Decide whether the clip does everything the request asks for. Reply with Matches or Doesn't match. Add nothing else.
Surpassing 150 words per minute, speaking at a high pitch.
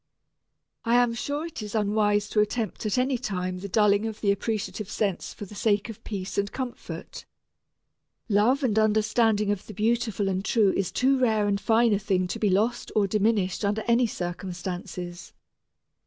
Matches